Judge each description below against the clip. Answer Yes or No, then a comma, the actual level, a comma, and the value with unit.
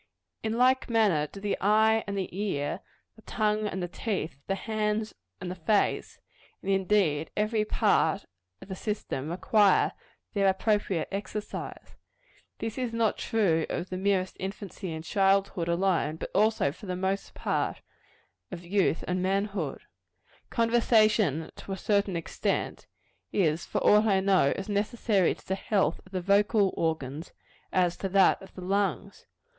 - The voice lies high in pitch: Yes, high, 195 Hz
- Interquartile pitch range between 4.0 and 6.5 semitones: No, average, 2.8 semitones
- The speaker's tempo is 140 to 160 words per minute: Yes, average, 155 wpm